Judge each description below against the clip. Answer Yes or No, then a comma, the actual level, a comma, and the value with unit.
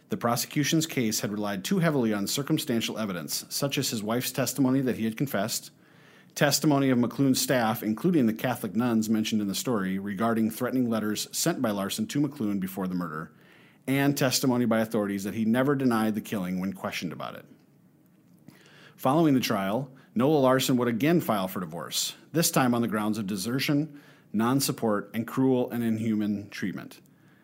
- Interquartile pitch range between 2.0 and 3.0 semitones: No, average, 4.4 semitones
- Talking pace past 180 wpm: No, average, 175 wpm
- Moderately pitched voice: No, low, 120 Hz